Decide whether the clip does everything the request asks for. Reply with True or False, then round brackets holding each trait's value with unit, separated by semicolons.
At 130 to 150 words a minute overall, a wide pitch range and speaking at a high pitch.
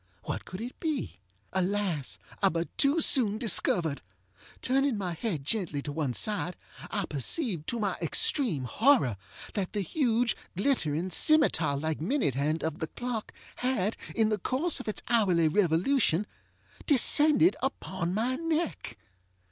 True (140 wpm; 8.0 semitones; 205 Hz)